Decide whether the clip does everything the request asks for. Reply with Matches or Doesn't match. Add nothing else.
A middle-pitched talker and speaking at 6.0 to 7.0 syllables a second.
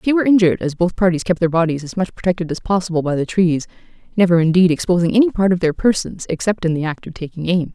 Matches